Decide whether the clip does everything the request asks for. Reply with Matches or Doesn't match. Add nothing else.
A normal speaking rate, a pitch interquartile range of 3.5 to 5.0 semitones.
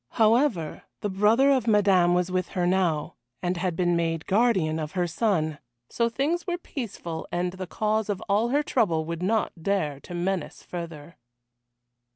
Matches